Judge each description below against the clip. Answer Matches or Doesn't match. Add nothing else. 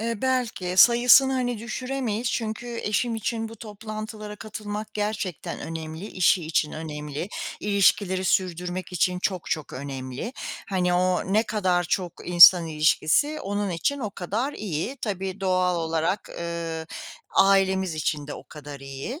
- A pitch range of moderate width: Matches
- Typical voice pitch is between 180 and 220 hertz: Matches